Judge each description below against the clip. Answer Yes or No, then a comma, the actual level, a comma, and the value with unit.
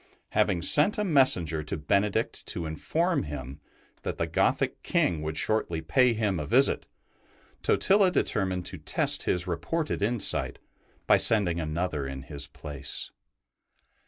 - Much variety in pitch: Yes, wide, 6.8 semitones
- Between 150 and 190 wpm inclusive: No, average, 140 wpm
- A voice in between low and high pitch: No, very low, 90 Hz